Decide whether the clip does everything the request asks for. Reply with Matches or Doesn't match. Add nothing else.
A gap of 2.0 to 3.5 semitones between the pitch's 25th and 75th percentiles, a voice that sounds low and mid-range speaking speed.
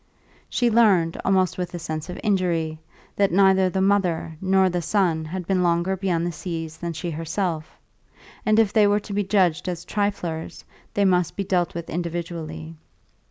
Doesn't match